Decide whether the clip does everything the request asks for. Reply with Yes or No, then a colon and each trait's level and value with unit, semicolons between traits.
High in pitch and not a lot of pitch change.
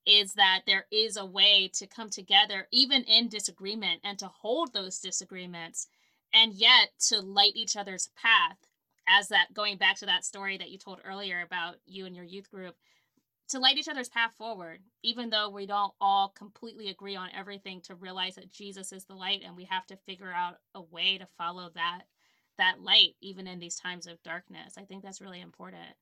Yes: high, 195 Hz; narrow, 2.1 semitones